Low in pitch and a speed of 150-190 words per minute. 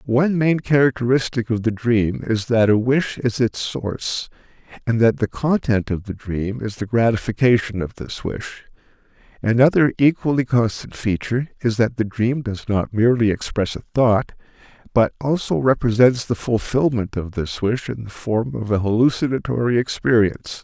Yes: low, 115 Hz; average, 160 wpm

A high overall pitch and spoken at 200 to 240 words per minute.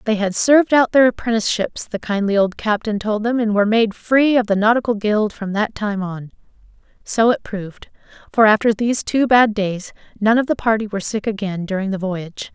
Yes: high, 215 Hz; fast, 205 wpm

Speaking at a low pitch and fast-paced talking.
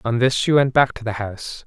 Yes: low, 120 Hz; fast, 290 wpm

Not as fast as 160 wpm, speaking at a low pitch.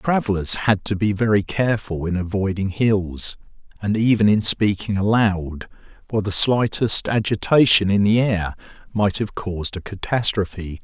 Yes: average, 150 wpm; low, 100 Hz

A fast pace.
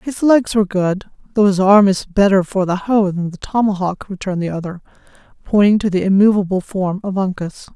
No: average, 195 wpm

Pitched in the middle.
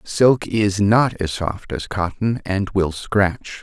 No: low, 100 Hz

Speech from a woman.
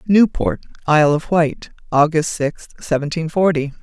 Yes: female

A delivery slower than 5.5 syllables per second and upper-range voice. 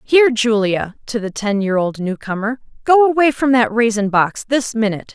Yes: 5.2 syllables/s; high, 225 Hz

